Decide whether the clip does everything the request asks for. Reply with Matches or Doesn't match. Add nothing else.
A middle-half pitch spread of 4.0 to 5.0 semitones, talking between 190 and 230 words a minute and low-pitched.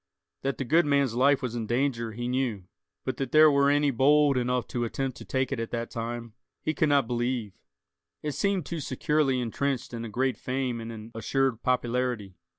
Doesn't match